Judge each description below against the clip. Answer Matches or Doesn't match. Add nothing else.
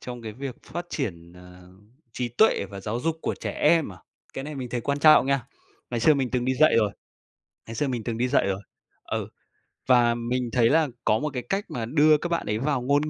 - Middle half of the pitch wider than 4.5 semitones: Doesn't match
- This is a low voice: Matches